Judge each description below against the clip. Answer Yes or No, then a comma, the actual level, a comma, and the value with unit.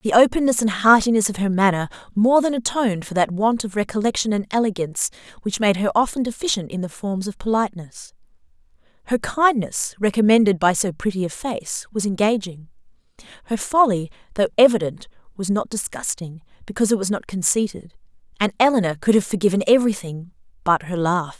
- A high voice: Yes, high, 205 Hz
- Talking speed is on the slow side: No, average, 165 wpm